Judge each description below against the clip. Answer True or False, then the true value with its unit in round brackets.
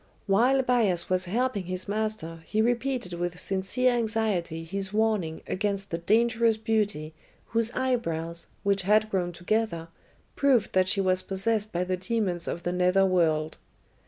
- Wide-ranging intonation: False (4.0 semitones)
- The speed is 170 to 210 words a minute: False (150 wpm)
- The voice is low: False (195 Hz)